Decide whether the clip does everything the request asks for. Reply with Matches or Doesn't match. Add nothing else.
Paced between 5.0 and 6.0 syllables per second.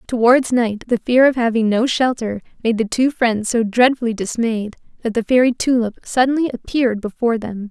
Matches